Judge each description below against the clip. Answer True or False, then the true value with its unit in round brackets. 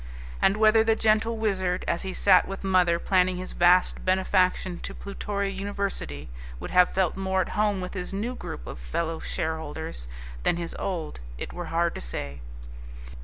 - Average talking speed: True (170 wpm)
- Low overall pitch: False (185 Hz)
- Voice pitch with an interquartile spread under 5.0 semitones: True (2.7 semitones)